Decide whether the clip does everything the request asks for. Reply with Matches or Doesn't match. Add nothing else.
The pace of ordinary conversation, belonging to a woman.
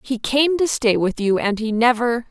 Doesn't match